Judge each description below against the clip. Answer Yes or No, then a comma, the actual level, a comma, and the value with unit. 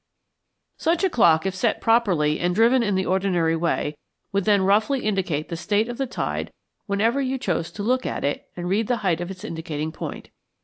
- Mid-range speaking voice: No, high, 195 Hz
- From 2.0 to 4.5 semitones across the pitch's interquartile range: No, average, 5.0 semitones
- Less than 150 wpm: No, fast, 205 wpm